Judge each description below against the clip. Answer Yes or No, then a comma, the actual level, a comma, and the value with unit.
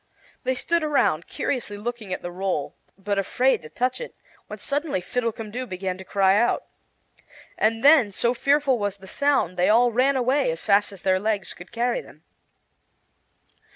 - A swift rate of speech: No, average, 170 wpm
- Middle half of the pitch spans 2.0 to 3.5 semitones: No, average, 5.1 semitones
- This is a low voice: No, high, 225 Hz